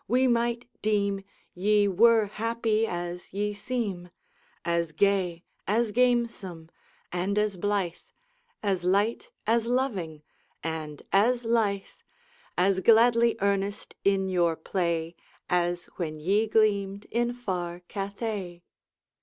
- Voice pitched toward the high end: Yes, high, 200 Hz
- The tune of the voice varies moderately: Yes, average, 4.2 semitones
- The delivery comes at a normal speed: No, slow, 110 wpm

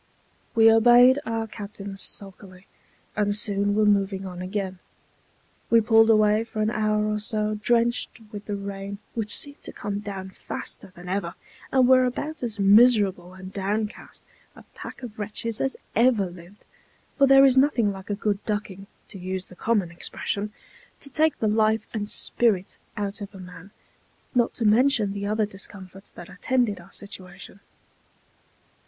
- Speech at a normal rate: Yes, average, 165 wpm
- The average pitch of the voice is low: No, high, 210 Hz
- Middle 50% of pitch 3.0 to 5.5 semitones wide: No, narrow, 2.5 semitones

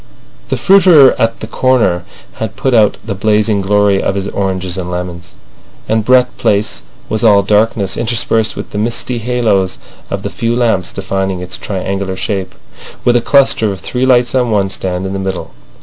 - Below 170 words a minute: No, average, 180 wpm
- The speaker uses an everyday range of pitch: Yes, average, 3.7 semitones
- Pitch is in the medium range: No, low, 105 Hz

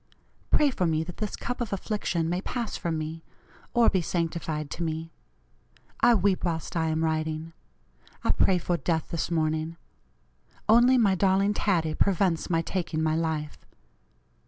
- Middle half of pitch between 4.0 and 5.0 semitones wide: No, average, 3.6 semitones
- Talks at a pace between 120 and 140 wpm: No, average, 160 wpm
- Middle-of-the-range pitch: Yes, medium, 170 Hz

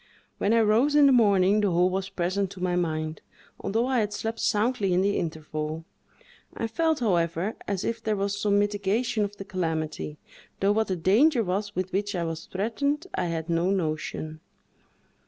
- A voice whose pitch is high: Yes, high, 195 Hz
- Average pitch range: Yes, average, 3.9 semitones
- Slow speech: No, average, 185 wpm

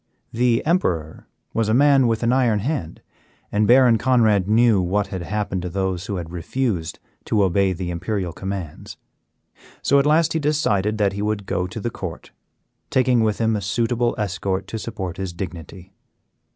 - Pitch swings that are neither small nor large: Yes, average, 4.2 semitones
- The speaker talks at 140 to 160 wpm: No, average, 175 wpm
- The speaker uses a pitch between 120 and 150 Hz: No, low, 105 Hz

